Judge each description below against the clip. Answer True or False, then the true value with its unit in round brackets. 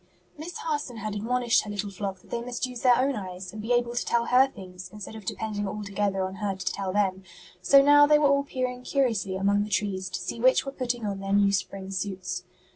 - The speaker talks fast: True (240 wpm)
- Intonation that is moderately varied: True (4.3 semitones)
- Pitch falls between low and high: False (210 Hz)